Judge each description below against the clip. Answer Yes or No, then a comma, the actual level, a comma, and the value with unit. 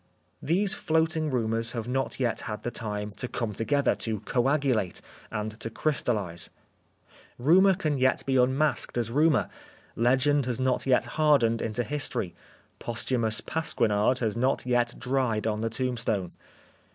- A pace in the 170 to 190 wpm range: No, average, 145 wpm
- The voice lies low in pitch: Yes, low, 125 Hz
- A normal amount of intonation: Yes, average, 3.6 semitones